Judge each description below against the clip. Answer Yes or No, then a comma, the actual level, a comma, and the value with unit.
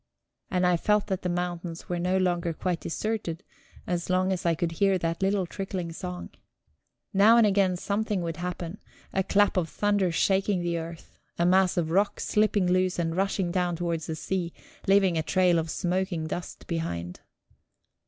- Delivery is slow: No, average, 175 wpm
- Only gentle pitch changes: Yes, narrow, 2.2 semitones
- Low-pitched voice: No, medium, 180 Hz